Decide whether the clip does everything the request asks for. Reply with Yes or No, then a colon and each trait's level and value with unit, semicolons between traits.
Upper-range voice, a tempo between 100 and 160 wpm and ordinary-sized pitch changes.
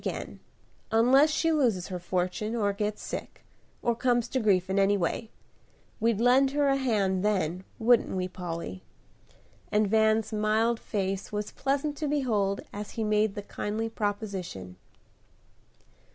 Yes: high, 215 Hz; average, 145 wpm; average, 3.4 semitones